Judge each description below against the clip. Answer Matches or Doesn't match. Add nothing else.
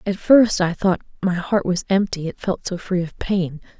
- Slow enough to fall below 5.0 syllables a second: Matches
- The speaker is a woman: Matches